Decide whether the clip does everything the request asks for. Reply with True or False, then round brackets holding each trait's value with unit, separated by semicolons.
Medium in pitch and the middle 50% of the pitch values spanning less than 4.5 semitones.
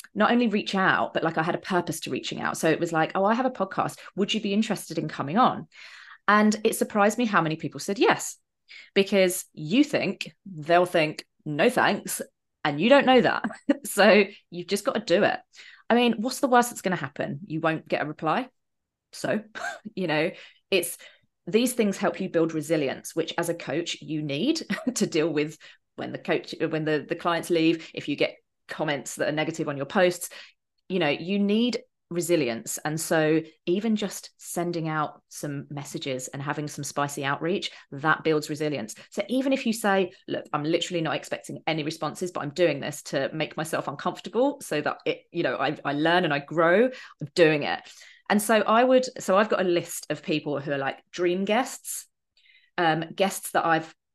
False (175 Hz; 5.1 semitones)